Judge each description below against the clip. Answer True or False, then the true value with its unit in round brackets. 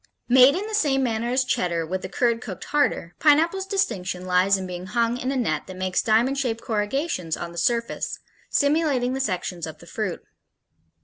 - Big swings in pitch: True (6.7 semitones)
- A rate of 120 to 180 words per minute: False (190 wpm)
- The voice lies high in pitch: True (230 Hz)